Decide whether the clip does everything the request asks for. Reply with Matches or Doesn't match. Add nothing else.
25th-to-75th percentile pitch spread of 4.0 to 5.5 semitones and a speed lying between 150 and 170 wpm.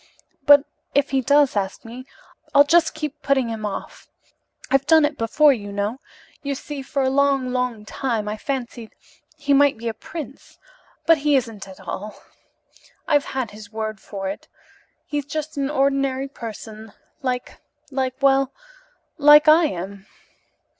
Matches